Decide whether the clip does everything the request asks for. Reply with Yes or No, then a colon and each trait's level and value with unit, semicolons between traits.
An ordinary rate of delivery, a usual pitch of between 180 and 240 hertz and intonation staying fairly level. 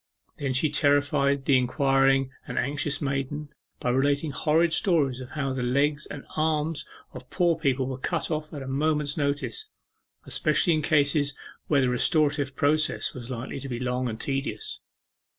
No: average, 165 wpm; medium, 140 Hz; narrow, 2.3 semitones